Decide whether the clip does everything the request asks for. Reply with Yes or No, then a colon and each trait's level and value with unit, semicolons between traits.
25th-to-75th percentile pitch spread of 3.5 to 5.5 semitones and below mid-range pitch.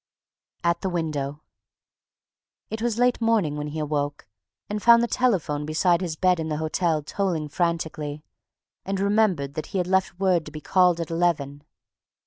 No: average, 4.1 semitones; medium, 170 Hz